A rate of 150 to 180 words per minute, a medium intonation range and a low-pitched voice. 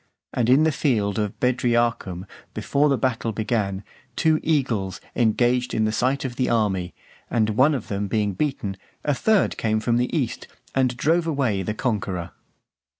Yes: average, 165 wpm; average, 4.3 semitones; low, 120 Hz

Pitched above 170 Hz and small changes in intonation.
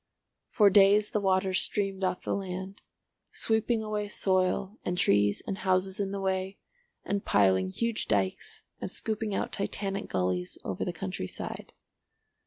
Yes: high, 190 Hz; narrow, 2.0 semitones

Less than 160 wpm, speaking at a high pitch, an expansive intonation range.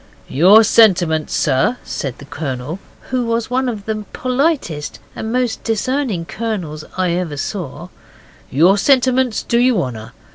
Yes: average, 140 wpm; high, 205 Hz; wide, 7.6 semitones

